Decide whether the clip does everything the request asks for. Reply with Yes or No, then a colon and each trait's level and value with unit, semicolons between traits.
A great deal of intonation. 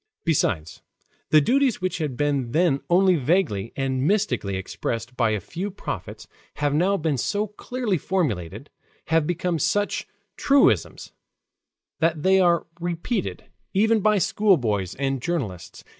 Yes: wide, 6.8 semitones